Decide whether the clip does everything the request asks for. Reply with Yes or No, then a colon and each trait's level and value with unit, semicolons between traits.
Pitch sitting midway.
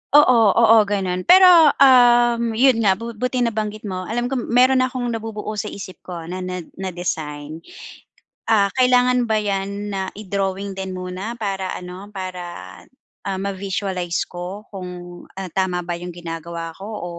No: high, 195 Hz